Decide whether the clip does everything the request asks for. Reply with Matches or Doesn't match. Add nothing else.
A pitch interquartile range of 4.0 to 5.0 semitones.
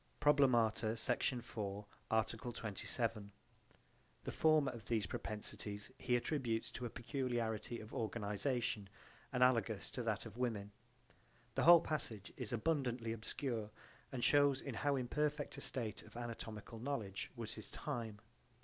Doesn't match